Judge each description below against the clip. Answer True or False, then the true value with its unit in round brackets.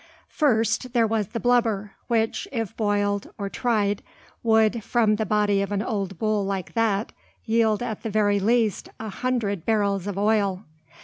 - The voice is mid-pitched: False (215 Hz)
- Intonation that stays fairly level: True (2.0 semitones)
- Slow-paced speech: False (165 wpm)